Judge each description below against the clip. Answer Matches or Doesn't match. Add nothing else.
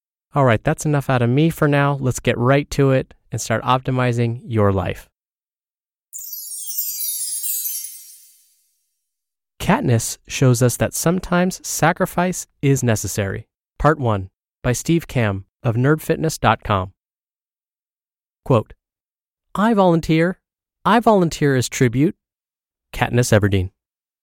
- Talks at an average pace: Doesn't match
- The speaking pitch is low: Matches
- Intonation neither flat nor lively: Doesn't match